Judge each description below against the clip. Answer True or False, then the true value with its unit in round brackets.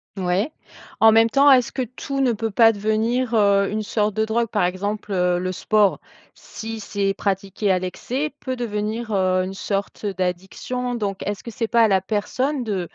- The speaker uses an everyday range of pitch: True (3.2 semitones)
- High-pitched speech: True (210 Hz)